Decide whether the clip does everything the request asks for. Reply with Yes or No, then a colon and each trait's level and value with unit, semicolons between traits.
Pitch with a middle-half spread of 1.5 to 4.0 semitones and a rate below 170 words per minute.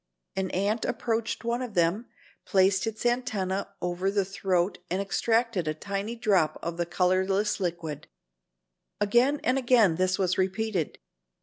Yes: average, 3.5 semitones; average, 140 wpm